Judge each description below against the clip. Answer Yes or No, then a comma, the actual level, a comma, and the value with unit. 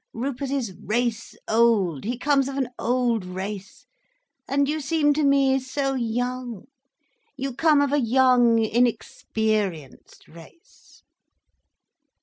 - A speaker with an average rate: No, slow, 115 wpm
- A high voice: Yes, very high, 250 Hz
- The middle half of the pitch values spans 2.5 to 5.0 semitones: Yes, average, 3.9 semitones